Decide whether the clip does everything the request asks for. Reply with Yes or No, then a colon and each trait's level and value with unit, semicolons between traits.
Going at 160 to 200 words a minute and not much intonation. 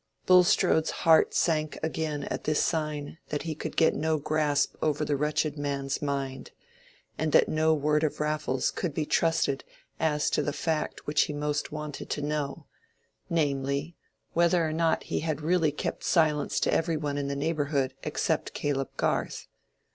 Yes: average, 165 wpm; narrow, 1.7 semitones